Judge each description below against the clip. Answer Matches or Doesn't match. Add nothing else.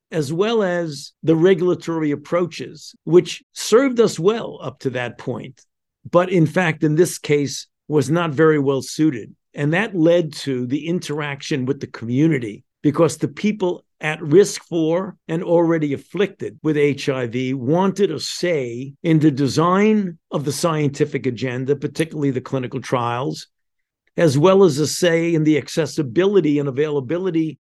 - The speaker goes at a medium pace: Matches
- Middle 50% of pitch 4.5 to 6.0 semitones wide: Doesn't match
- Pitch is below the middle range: Doesn't match